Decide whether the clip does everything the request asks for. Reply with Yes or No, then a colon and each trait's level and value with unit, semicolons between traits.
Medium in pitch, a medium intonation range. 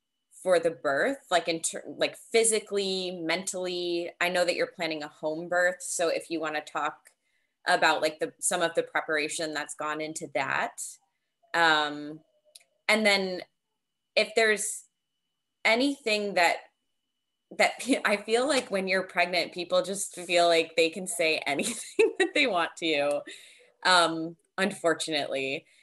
Yes: medium, 175 Hz; average, 4.2 semitones